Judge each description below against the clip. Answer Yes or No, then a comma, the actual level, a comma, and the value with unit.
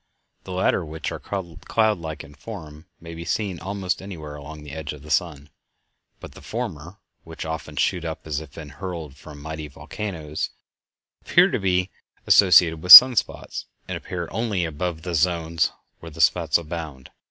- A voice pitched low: Yes, very low, 80 Hz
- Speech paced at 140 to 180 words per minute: Yes, average, 165 wpm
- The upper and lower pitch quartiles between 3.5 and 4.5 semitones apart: No, average, 3.0 semitones